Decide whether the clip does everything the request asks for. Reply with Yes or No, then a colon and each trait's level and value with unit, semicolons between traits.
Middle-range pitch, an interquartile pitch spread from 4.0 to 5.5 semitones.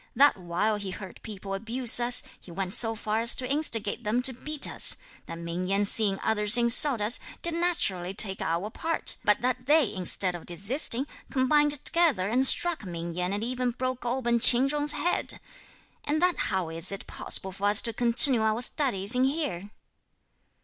No: high, 230 Hz; average, 5.1 semitones